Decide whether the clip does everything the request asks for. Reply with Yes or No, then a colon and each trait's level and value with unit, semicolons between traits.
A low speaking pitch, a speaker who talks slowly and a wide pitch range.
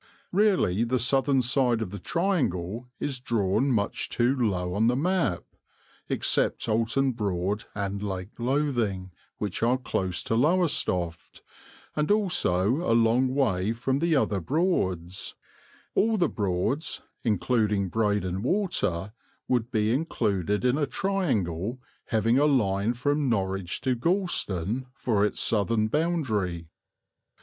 Yes: low, 115 Hz; slow, 125 wpm; wide, 5.8 semitones